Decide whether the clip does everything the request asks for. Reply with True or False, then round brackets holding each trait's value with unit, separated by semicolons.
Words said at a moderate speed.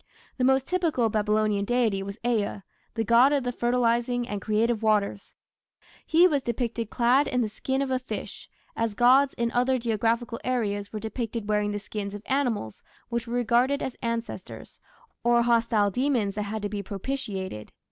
True (170 wpm)